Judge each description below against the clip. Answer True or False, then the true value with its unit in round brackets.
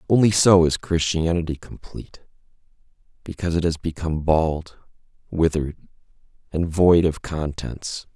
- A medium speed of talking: False (110 wpm)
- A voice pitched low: True (80 Hz)